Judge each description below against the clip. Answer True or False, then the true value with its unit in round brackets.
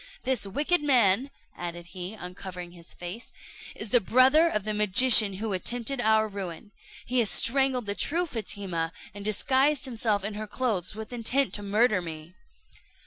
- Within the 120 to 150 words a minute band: False (160 wpm)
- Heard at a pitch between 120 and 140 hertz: False (215 Hz)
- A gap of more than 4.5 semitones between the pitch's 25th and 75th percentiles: True (5.0 semitones)